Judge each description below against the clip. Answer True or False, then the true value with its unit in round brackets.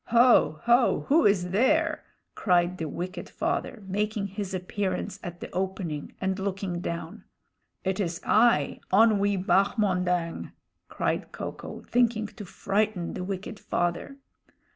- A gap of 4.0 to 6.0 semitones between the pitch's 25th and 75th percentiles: False (3.0 semitones)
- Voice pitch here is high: True (195 Hz)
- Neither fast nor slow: False (130 wpm)